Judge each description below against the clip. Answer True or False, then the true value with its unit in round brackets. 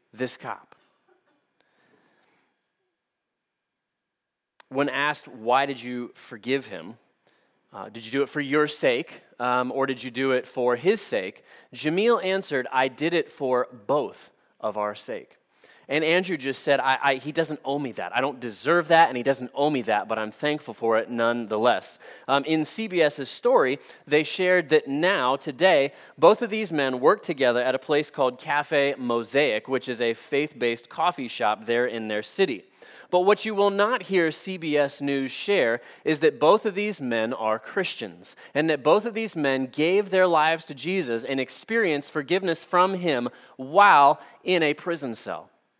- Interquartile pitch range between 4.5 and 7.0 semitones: True (4.8 semitones)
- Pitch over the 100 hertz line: True (140 Hz)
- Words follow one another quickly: False (175 wpm)